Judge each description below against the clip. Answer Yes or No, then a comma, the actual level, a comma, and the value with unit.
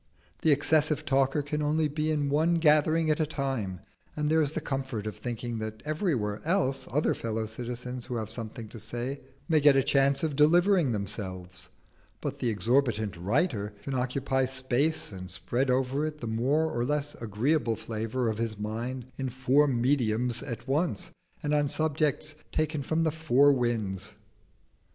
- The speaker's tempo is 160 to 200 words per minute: Yes, average, 170 wpm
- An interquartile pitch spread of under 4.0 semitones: No, average, 4.6 semitones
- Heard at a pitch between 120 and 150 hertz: Yes, low, 135 Hz